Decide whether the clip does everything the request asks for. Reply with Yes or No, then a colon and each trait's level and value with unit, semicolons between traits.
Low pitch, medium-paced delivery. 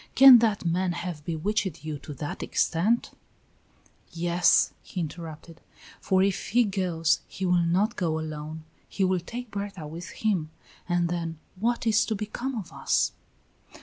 No: medium, 180 Hz; average, 155 wpm